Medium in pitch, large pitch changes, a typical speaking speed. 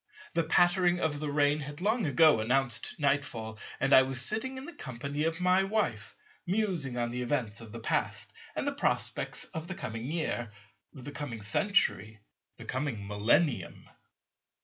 Yes: medium, 145 Hz; wide, 6.5 semitones; average, 165 wpm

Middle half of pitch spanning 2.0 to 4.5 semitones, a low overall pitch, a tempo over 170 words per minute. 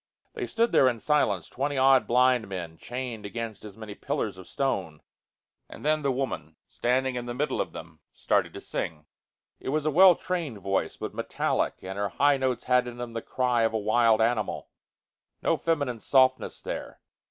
Yes: average, 3.9 semitones; low, 125 Hz; average, 185 wpm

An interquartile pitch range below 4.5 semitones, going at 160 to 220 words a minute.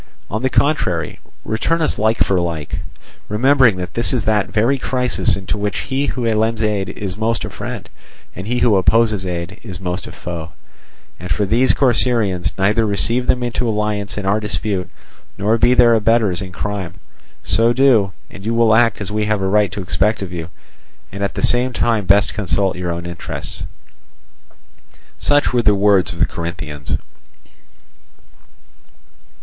Yes: average, 3.7 semitones; average, 165 wpm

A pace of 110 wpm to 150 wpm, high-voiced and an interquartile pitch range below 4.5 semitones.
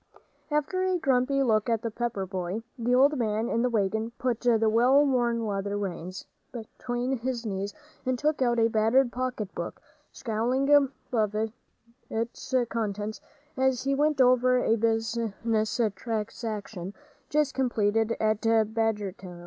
Yes: average, 140 wpm; high, 230 Hz; average, 2.9 semitones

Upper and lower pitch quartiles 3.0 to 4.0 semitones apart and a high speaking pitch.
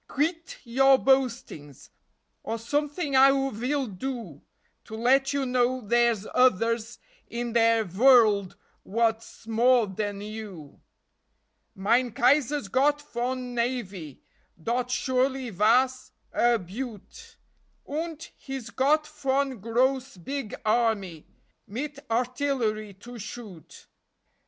Yes: average, 3.6 semitones; high, 240 Hz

